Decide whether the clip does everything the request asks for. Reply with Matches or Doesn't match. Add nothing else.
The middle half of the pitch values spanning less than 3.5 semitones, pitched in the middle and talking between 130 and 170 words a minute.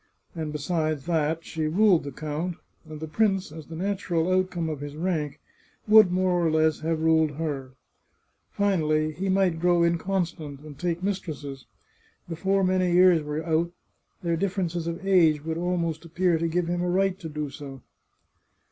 Matches